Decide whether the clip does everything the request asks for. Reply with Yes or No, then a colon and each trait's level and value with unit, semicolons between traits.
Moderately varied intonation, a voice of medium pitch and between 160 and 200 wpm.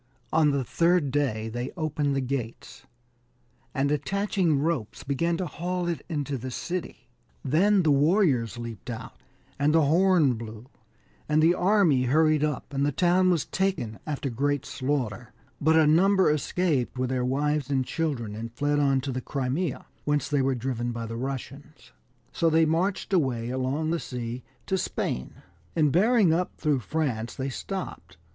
Yes: average, 4.3 semitones; medium, 145 Hz; average, 165 wpm